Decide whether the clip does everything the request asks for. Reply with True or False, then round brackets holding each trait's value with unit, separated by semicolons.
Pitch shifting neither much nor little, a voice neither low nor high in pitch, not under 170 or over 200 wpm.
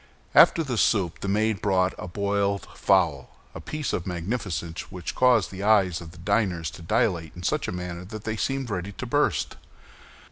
False (3.6 semitones; 95 Hz; 180 wpm)